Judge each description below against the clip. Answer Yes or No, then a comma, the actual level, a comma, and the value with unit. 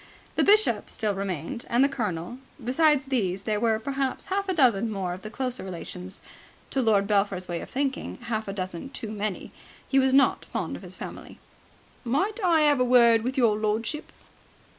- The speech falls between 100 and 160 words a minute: No, average, 185 wpm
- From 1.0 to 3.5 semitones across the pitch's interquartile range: No, average, 5.2 semitones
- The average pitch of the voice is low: No, high, 230 Hz